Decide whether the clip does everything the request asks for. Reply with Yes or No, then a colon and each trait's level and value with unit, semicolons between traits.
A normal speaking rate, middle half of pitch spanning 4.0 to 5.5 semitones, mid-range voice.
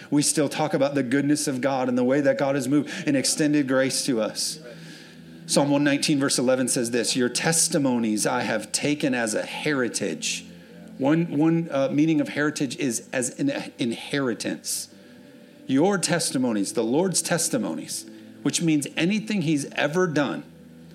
Yes: average, 160 wpm; average, 4.3 semitones; medium, 150 Hz